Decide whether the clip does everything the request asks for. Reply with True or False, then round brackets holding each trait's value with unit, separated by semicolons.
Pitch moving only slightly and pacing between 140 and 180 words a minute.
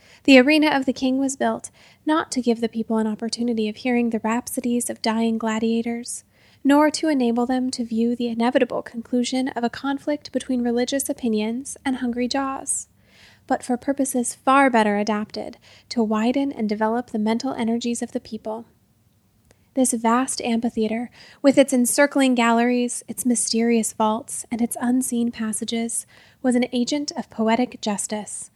True (2.3 semitones; 160 wpm)